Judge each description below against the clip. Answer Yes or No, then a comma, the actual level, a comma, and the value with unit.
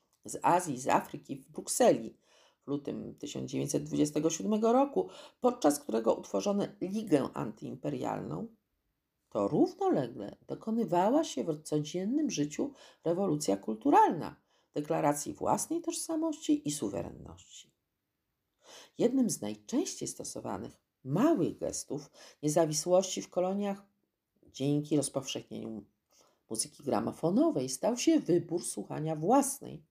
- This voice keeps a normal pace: No, slow, 95 wpm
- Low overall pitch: No, medium, 175 Hz